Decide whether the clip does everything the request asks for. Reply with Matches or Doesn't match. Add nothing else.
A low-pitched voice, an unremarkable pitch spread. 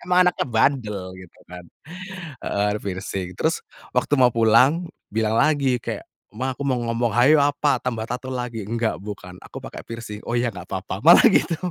Matches